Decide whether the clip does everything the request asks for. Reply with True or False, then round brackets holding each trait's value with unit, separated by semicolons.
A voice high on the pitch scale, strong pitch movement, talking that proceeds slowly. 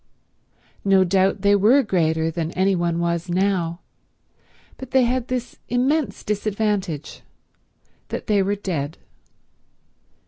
False (195 Hz; 4.0 semitones; 115 wpm)